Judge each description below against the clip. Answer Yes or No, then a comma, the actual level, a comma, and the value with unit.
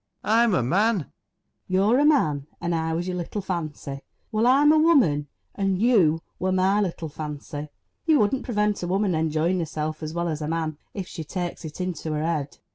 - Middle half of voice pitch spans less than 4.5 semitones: No, average, 5.0 semitones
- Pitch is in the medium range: Yes, medium, 175 Hz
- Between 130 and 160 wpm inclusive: No, average, 200 wpm